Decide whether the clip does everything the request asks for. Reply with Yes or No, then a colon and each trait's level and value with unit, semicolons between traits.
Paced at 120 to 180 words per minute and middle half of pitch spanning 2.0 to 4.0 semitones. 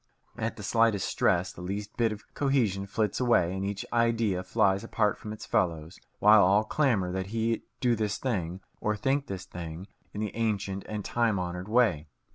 No: average, 190 wpm; average, 3.4 semitones